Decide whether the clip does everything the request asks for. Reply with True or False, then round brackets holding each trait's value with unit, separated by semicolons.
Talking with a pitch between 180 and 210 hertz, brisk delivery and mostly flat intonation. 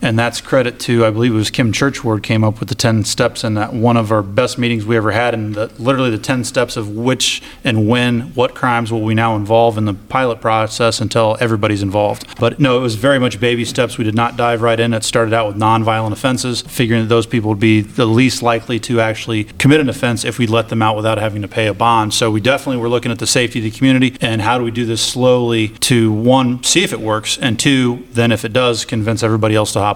False (115 Hz; 260 wpm; 1.9 semitones)